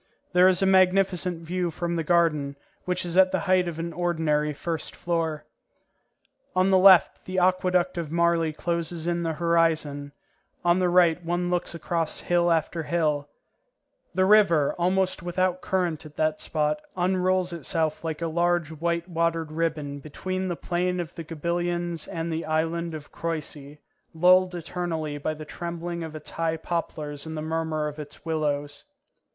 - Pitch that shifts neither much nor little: No, narrow, 2.1 semitones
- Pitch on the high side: No, medium, 170 Hz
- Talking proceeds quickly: No, average, 165 wpm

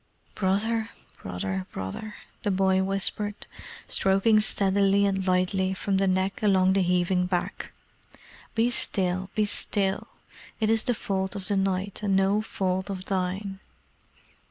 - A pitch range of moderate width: No, narrow, 1.5 semitones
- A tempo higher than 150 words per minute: No, slow, 135 wpm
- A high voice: Yes, high, 195 Hz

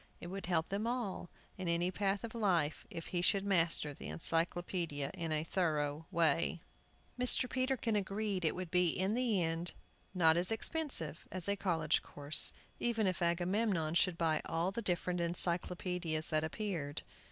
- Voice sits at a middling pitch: Yes, medium, 175 Hz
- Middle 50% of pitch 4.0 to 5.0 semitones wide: No, average, 3.4 semitones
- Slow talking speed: No, average, 165 wpm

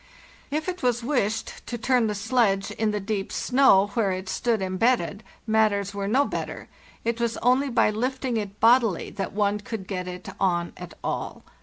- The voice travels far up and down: No, average, 3.7 semitones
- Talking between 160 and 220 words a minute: Yes, average, 180 wpm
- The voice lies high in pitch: Yes, high, 220 Hz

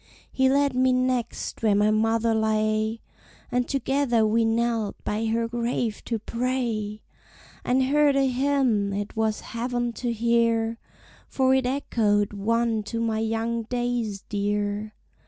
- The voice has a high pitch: Yes, high, 230 Hz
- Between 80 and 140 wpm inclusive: Yes, slow, 135 wpm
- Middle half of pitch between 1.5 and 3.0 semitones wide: Yes, narrow, 2.4 semitones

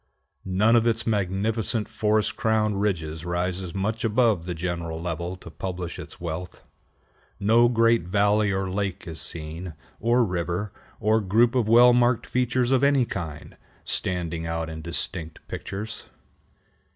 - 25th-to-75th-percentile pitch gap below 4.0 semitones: No, average, 4.6 semitones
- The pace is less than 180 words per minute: Yes, average, 140 wpm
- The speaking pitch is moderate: No, low, 100 Hz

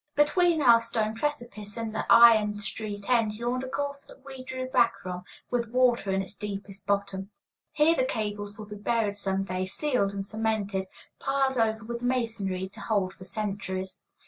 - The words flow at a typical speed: Yes, average, 175 wpm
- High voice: Yes, high, 220 Hz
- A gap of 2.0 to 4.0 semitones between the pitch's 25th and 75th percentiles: Yes, average, 3.7 semitones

